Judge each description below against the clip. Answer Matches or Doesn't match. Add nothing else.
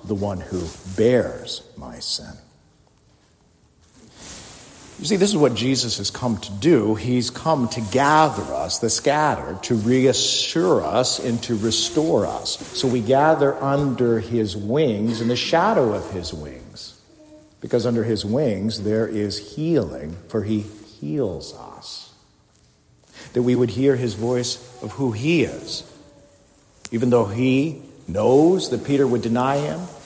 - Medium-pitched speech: Doesn't match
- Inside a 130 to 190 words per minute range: Matches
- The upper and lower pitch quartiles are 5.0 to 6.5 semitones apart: Doesn't match